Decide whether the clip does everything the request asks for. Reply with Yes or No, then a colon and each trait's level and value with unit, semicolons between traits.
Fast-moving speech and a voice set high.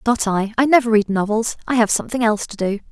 Yes: fast, 245 wpm; high, 220 Hz